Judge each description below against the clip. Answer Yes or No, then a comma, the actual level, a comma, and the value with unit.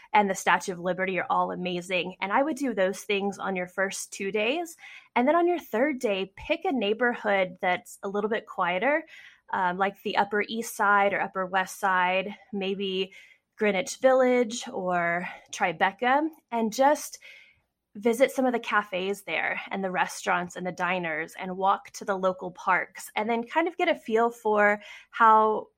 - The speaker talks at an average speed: Yes, average, 180 wpm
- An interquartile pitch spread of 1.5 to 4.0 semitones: No, average, 4.8 semitones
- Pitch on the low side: No, high, 205 Hz